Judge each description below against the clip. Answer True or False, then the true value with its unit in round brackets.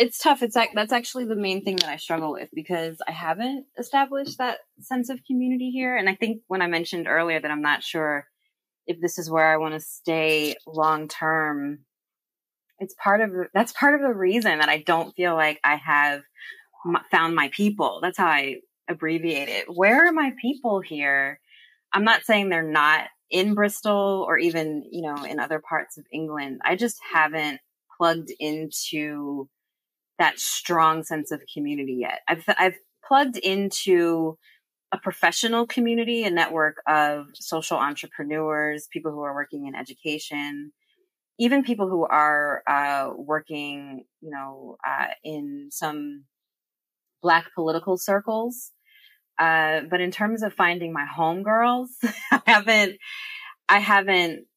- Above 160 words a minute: False (155 wpm)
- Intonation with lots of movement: True (6.4 semitones)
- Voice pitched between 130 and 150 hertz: False (170 Hz)